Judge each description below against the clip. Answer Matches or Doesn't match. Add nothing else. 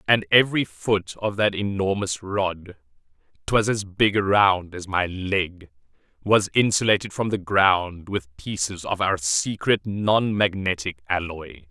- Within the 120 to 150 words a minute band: Matches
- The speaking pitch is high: Doesn't match